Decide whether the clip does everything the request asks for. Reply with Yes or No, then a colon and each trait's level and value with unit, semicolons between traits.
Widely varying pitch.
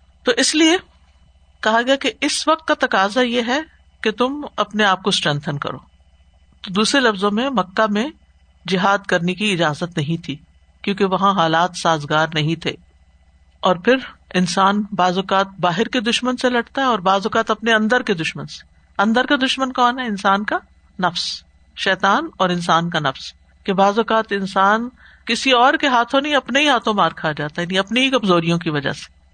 Yes: wide, 6.4 semitones